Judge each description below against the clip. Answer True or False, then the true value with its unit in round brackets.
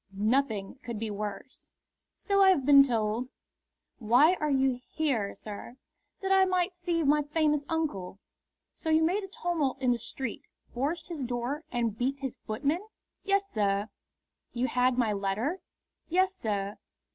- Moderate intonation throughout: False (6.3 semitones)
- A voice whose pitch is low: False (270 Hz)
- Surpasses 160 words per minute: False (155 wpm)